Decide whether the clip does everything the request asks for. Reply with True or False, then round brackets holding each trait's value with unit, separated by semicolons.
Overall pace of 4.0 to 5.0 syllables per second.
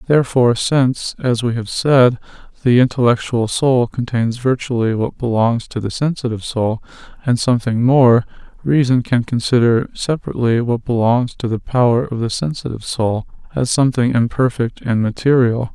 False (5.2 syllables/s)